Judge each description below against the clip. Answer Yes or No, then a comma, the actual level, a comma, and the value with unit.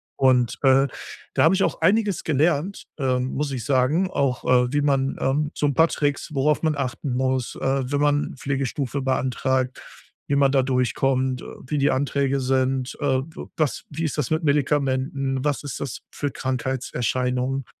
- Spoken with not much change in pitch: Yes, narrow, 2.0 semitones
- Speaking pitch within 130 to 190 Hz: Yes, low, 135 Hz